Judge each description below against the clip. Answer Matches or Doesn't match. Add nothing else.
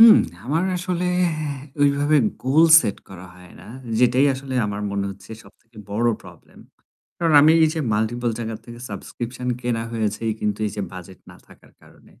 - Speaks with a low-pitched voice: Matches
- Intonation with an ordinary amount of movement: Doesn't match